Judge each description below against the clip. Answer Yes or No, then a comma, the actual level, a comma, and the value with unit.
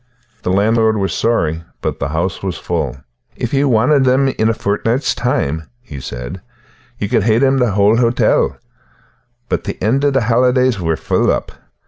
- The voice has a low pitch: Yes, low, 110 Hz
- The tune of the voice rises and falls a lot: Yes, wide, 6.1 semitones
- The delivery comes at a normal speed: Yes, average, 175 wpm